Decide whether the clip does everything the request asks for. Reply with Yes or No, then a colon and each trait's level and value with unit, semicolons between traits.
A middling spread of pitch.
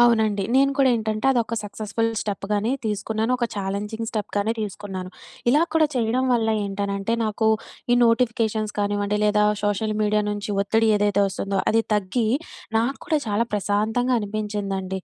No: narrow, 1.9 semitones